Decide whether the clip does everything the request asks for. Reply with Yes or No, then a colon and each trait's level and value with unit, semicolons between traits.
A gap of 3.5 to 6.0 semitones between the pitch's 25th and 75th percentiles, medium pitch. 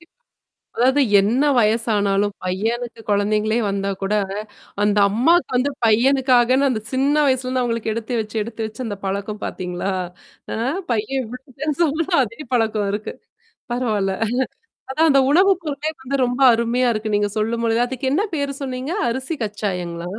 No: average, 3.9 semitones; high, 235 Hz